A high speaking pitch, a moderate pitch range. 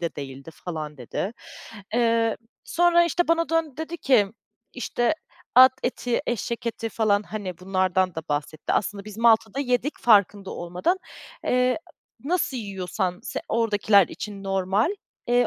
Yes: high, 220 Hz; average, 5.0 semitones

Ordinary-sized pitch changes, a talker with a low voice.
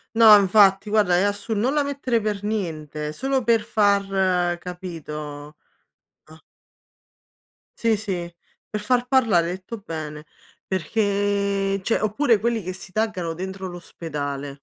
No: average, 4.0 semitones; high, 195 Hz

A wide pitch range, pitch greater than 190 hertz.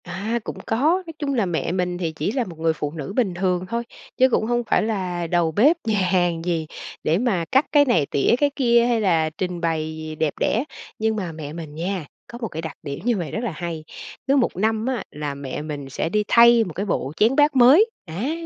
No: wide, 6.5 semitones; medium, 185 Hz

